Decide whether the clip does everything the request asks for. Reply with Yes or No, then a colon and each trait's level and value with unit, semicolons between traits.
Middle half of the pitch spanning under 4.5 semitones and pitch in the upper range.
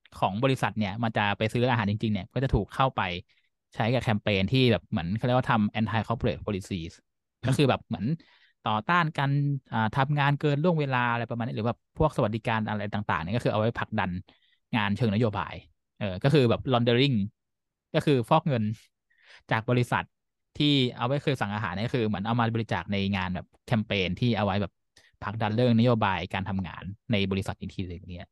No: average, 3.7 semitones; low, 115 Hz